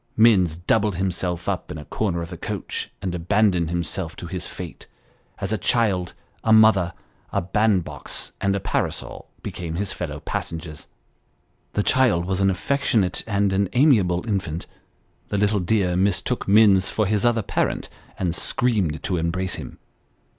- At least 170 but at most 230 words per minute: No, average, 155 wpm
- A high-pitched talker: No, very low, 95 Hz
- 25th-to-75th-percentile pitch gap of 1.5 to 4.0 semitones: Yes, average, 3.3 semitones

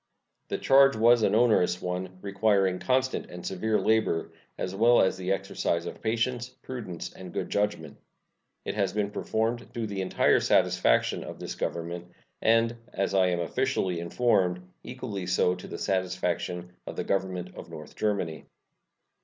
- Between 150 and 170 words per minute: Yes, average, 155 wpm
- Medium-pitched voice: No, low, 100 Hz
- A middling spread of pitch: Yes, average, 3.9 semitones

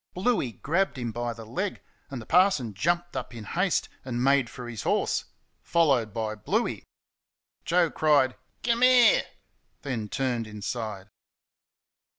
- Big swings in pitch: Yes, wide, 7.2 semitones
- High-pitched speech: No, low, 130 Hz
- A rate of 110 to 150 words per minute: Yes, average, 140 wpm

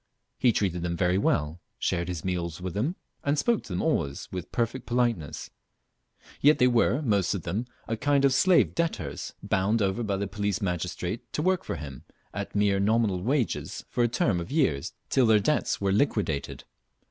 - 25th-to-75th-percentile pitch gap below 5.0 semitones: No, wide, 5.6 semitones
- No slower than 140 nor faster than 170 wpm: No, average, 185 wpm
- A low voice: Yes, low, 100 Hz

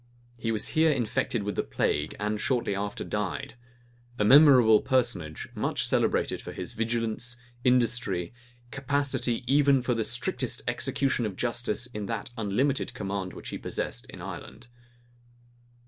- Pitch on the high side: No, low, 115 Hz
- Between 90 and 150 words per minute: Yes, average, 140 wpm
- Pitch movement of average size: Yes, average, 3.4 semitones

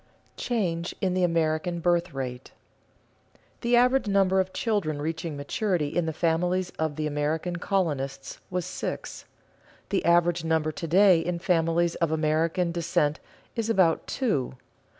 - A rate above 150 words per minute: No, average, 145 wpm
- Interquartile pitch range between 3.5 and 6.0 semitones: No, average, 2.7 semitones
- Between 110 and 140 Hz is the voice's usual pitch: No, medium, 170 Hz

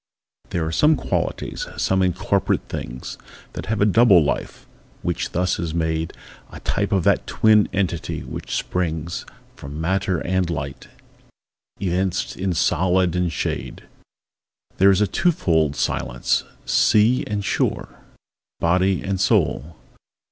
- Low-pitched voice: Yes, very low, 90 Hz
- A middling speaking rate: No, slow, 125 wpm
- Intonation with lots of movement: No, average, 3.1 semitones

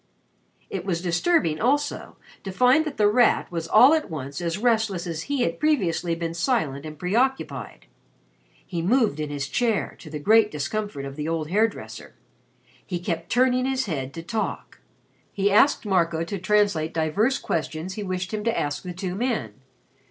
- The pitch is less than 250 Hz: Yes, medium, 185 Hz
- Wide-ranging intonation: Yes, wide, 5.9 semitones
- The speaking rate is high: No, average, 175 wpm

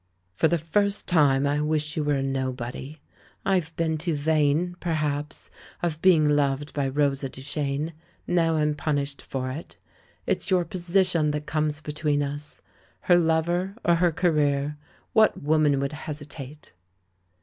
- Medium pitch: Yes, medium, 150 Hz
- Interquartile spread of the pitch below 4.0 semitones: Yes, narrow, 2.5 semitones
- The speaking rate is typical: Yes, average, 150 wpm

